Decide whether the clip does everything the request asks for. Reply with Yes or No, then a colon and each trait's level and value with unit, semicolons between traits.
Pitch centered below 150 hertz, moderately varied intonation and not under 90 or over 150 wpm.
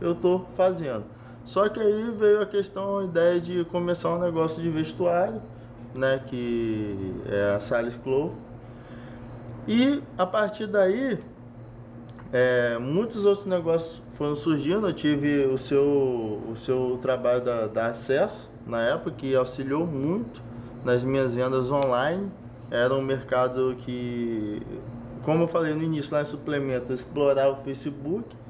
No: low, 135 Hz; wide, 5.7 semitones; average, 135 wpm